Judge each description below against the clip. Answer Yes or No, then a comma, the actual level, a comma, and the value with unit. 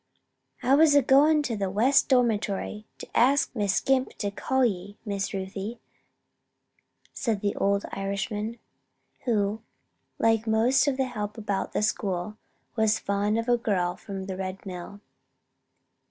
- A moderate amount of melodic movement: Yes, average, 3.4 semitones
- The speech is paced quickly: No, average, 150 wpm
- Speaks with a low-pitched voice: No, high, 210 Hz